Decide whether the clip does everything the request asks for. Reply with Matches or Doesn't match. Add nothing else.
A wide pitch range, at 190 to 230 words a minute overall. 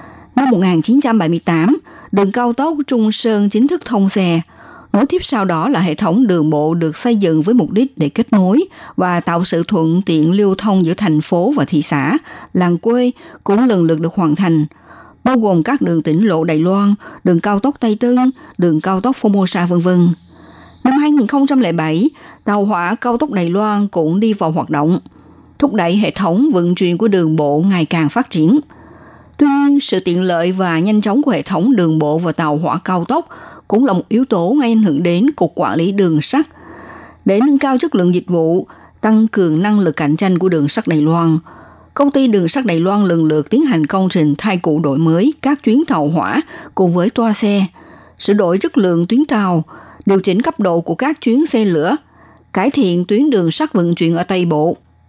Matches